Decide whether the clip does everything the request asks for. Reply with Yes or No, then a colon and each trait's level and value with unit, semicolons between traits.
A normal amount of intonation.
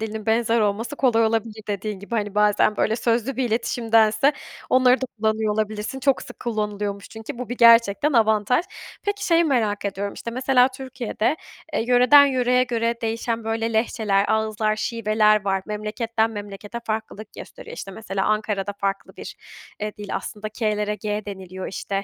No: narrow, 2.3 semitones